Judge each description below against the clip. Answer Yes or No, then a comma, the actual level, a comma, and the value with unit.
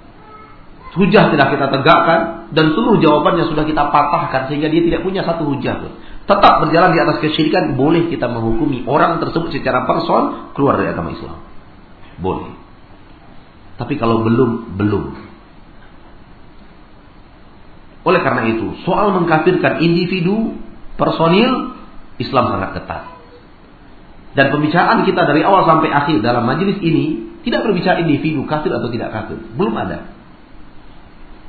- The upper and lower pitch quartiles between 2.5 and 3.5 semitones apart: No, average, 5.2 semitones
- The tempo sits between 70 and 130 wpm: Yes, average, 125 wpm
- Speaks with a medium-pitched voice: Yes, medium, 155 Hz